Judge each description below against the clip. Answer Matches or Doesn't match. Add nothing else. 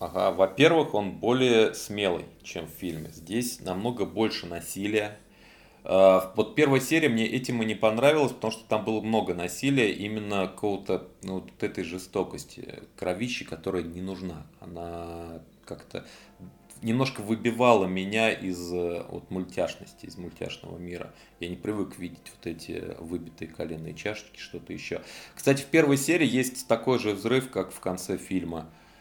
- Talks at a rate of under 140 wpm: Doesn't match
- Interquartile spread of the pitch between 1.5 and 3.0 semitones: Doesn't match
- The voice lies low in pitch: Matches